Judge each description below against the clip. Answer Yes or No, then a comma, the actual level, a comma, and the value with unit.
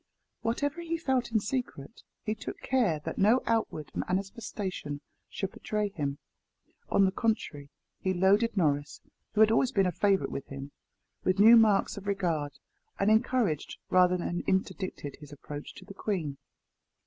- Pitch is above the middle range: Yes, high, 195 Hz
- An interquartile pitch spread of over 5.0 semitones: Yes, wide, 5.6 semitones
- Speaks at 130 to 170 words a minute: Yes, average, 155 wpm